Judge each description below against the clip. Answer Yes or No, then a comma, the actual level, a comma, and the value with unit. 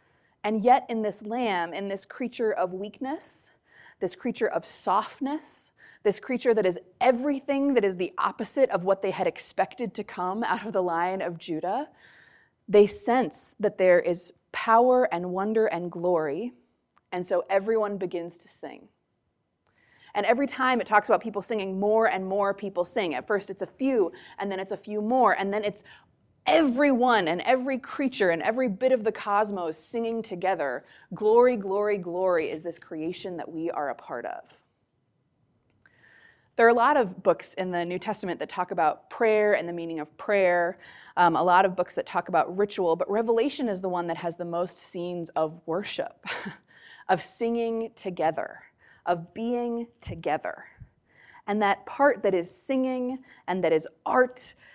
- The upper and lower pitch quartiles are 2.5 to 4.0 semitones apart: No, average, 4.7 semitones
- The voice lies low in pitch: No, high, 205 Hz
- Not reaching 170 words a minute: No, average, 175 wpm